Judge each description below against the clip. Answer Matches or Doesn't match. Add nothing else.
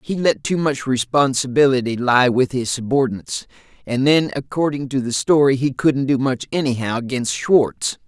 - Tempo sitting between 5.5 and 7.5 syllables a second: Doesn't match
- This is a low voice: Matches